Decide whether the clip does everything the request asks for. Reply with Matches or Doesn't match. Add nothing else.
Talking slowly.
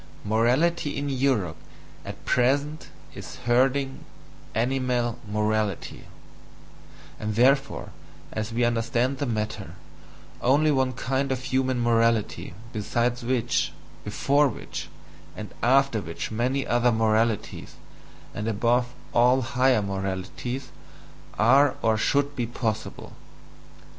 Matches